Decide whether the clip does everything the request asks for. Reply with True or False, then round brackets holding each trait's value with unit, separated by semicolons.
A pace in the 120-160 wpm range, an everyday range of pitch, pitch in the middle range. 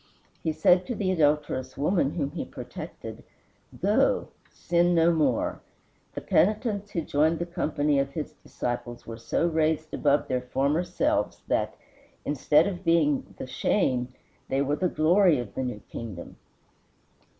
True (150 wpm; 4.0 semitones; 155 Hz)